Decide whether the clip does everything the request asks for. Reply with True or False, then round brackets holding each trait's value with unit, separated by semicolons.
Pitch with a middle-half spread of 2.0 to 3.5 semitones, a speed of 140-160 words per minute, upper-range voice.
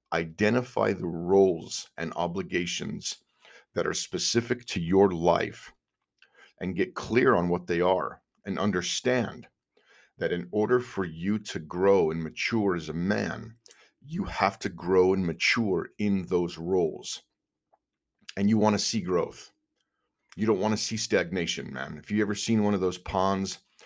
False (3.2 semitones; 155 wpm; 95 Hz)